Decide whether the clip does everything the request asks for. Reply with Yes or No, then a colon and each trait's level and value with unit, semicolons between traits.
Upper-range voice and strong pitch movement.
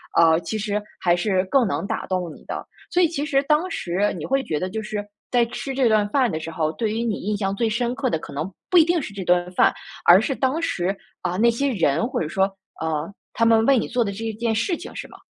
Yes: high, 215 Hz; wide, 5.9 semitones